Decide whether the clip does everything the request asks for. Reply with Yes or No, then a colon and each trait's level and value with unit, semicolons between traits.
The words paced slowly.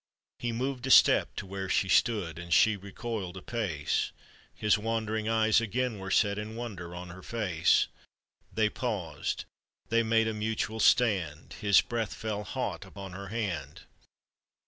No: average, 155 wpm